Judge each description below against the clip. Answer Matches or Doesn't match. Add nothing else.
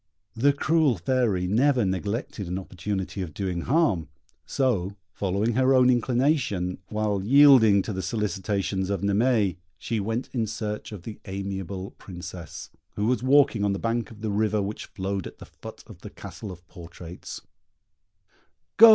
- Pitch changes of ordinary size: Matches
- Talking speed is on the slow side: Doesn't match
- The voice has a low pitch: Matches